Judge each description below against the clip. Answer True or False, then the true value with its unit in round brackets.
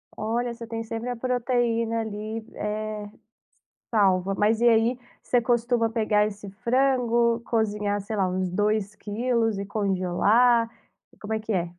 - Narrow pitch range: True (2.2 semitones)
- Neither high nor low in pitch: False (220 Hz)